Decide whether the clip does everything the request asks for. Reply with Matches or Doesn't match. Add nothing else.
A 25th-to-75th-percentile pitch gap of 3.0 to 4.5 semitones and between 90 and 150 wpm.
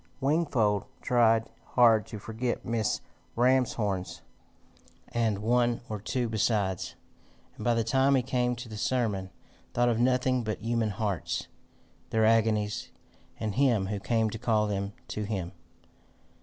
Doesn't match